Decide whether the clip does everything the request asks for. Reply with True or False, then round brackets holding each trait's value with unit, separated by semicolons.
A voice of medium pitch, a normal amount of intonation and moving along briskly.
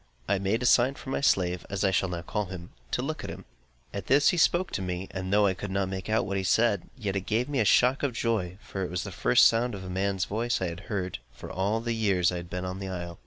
False (95 Hz; 3.6 semitones; 295 wpm)